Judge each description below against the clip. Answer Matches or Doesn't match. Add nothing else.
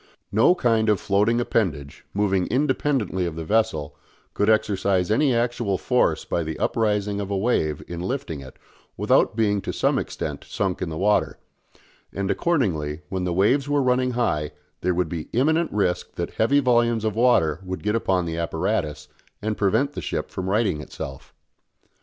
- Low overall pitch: Matches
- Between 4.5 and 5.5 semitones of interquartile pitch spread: Matches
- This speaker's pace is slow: Doesn't match